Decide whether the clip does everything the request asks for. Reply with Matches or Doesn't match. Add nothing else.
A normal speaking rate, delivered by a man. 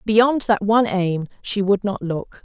Doesn't match